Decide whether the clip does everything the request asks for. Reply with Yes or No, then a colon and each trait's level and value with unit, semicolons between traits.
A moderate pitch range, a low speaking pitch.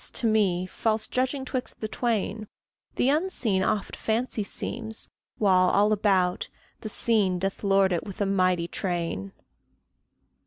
No: average, 3.2 semitones; high, 205 Hz